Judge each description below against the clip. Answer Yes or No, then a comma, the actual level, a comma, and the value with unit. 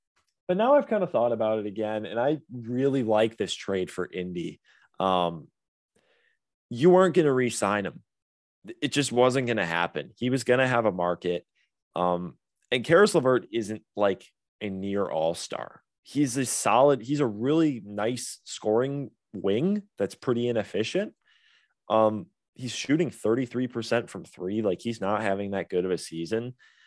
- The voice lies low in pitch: Yes, low, 120 Hz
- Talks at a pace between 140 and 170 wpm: Yes, average, 165 wpm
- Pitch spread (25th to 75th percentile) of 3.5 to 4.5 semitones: No, wide, 5.4 semitones